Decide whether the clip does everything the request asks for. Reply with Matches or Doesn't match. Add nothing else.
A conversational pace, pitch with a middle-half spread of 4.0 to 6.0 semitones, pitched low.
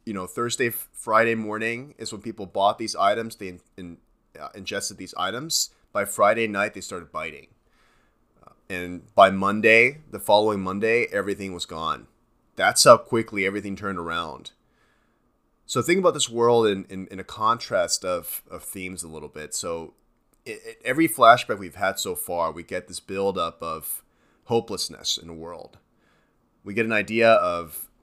Doesn't match